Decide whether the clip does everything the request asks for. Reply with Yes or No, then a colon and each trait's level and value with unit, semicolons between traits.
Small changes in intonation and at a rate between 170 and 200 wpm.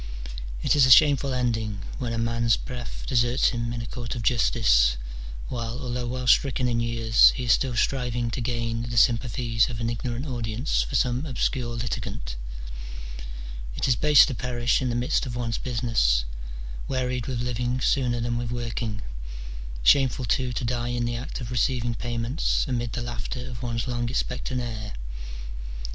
Yes: narrow, 1.4 semitones; average, 175 wpm